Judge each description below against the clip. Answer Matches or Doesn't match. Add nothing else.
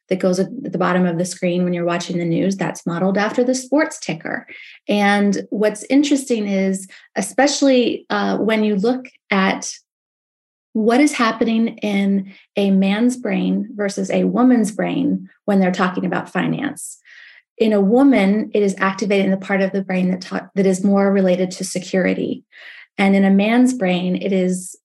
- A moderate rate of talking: Matches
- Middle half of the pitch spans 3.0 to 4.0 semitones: Matches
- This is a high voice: Matches